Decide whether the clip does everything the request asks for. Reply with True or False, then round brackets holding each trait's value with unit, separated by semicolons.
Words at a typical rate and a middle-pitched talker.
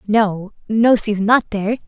False (160 wpm; 215 Hz)